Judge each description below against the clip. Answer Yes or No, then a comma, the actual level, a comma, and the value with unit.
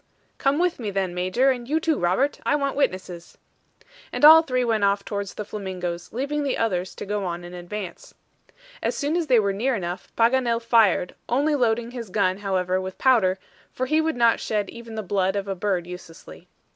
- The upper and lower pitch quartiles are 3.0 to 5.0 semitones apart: No, wide, 5.6 semitones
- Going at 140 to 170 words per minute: No, average, 200 wpm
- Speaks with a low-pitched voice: No, high, 210 Hz